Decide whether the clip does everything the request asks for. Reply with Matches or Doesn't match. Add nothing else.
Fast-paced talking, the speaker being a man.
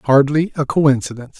Doesn't match